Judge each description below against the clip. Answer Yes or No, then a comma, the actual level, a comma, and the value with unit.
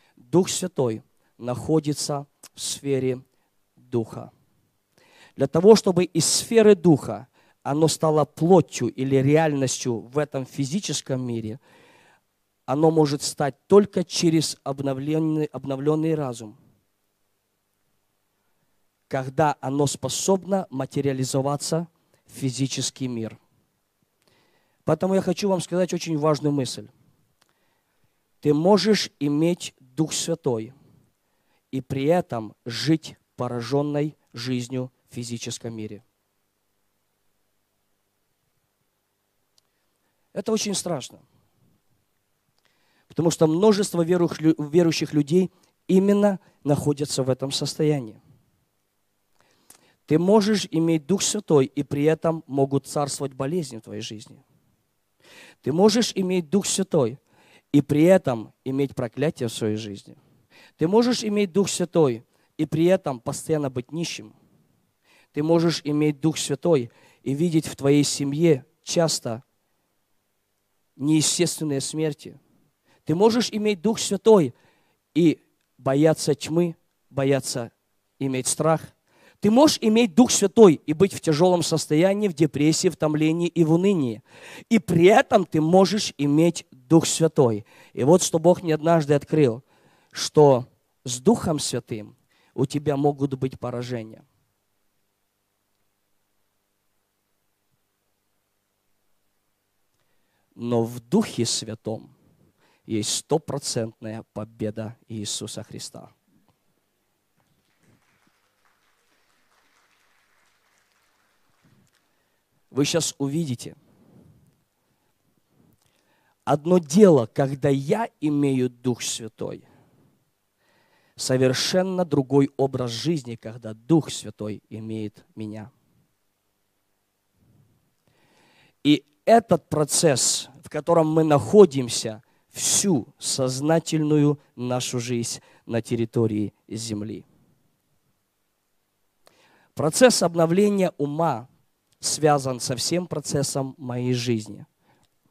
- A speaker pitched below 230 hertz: Yes, medium, 140 Hz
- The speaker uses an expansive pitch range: Yes, wide, 5.8 semitones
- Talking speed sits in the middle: No, slow, 95 wpm